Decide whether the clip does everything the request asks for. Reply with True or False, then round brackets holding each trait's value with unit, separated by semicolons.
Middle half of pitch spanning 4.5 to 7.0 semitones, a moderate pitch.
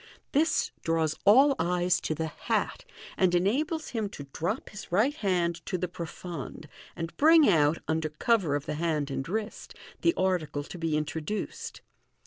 True (4.9 semitones; 175 Hz)